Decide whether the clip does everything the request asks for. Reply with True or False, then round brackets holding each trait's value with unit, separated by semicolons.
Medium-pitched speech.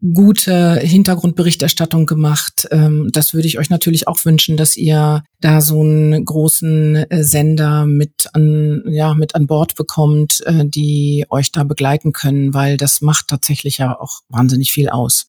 True (155 Hz)